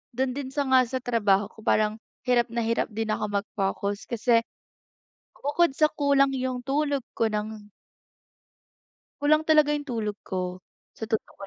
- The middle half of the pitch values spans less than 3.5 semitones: No, average, 4.8 semitones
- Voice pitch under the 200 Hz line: No, high, 235 Hz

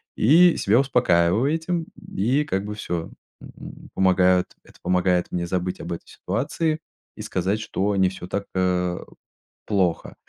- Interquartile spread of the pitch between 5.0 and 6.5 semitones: Yes, wide, 5.5 semitones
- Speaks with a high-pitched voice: No, very low, 95 Hz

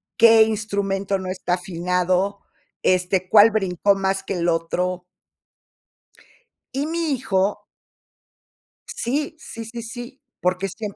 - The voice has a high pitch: Yes, high, 195 Hz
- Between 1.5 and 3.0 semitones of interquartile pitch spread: No, average, 3.6 semitones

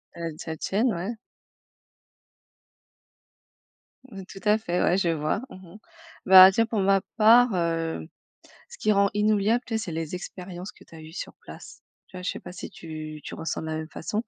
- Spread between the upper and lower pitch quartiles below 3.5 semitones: No, average, 4.2 semitones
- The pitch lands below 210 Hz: Yes, medium, 185 Hz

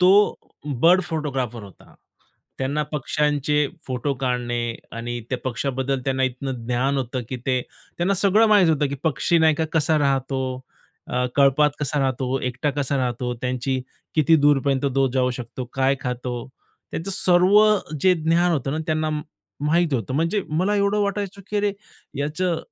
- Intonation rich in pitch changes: No, average, 4.2 semitones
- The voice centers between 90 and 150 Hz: Yes, medium, 140 Hz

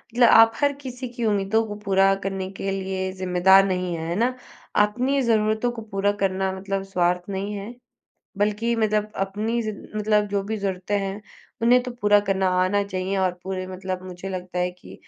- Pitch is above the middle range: Yes, high, 195 Hz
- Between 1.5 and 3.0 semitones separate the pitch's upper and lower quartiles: Yes, narrow, 2.4 semitones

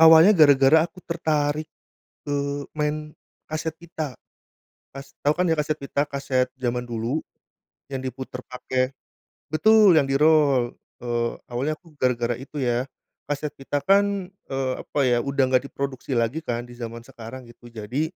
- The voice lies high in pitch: No, medium, 140 Hz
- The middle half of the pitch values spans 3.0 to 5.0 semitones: Yes, average, 3.5 semitones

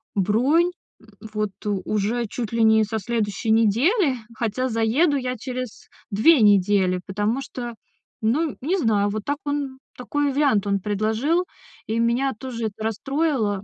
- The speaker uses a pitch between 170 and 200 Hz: No, high, 230 Hz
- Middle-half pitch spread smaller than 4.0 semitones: No, average, 4.4 semitones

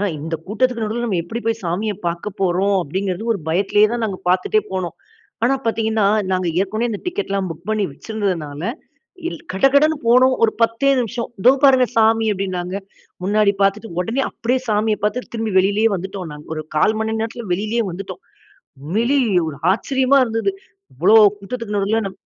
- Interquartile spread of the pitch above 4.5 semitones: No, average, 3.5 semitones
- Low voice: No, high, 210 Hz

